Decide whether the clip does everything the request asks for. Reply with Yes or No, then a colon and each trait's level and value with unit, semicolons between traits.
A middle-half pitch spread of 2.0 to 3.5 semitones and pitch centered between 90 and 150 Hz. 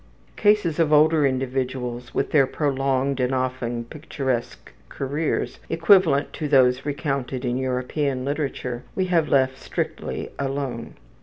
Yes: average, 2.8 semitones; low, 135 Hz